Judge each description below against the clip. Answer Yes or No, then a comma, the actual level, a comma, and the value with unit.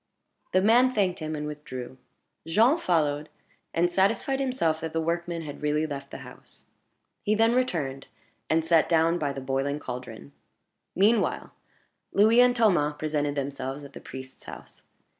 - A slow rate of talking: No, average, 155 wpm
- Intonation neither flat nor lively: No, wide, 5.7 semitones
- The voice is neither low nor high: Yes, medium, 160 Hz